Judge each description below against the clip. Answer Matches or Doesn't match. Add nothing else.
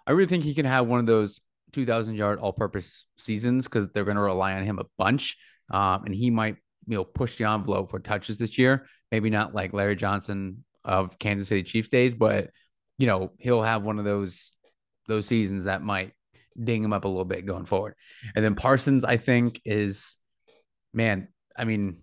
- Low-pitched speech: Matches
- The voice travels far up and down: Doesn't match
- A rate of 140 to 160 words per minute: Doesn't match